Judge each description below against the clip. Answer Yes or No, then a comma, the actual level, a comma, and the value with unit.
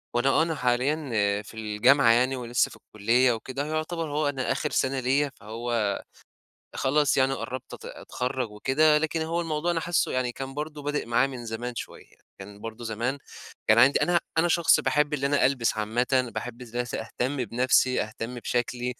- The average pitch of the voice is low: Yes, low, 130 Hz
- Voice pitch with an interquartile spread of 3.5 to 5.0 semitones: Yes, average, 3.8 semitones